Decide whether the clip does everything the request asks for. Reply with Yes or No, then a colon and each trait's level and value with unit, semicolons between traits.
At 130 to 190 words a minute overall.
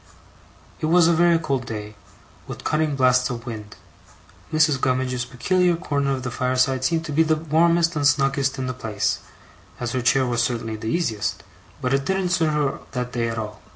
No: average, 200 wpm